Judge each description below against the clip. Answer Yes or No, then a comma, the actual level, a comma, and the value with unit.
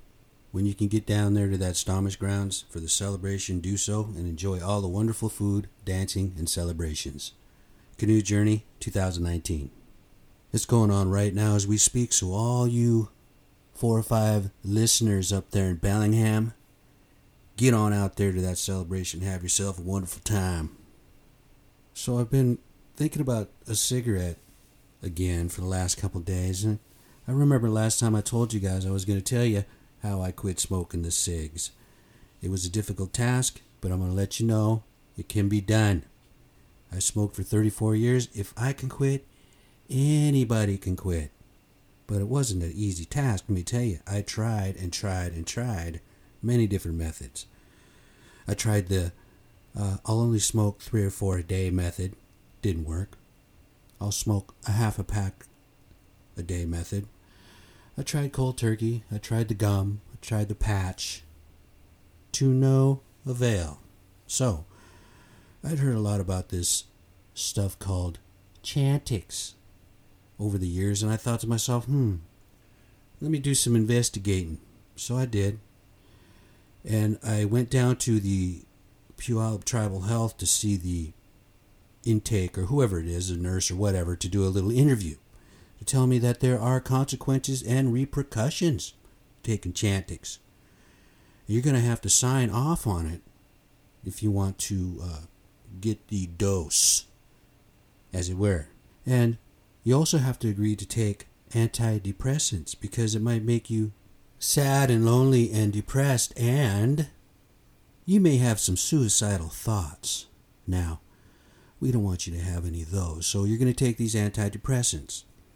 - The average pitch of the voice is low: Yes, low, 105 Hz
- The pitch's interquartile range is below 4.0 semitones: Yes, average, 3.5 semitones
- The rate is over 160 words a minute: No, average, 155 wpm